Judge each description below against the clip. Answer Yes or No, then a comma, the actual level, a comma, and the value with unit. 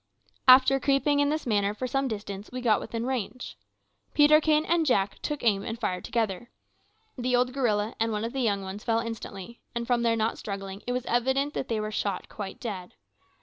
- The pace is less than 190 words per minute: No, average, 200 wpm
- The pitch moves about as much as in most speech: Yes, average, 3.9 semitones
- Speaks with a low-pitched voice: No, high, 235 Hz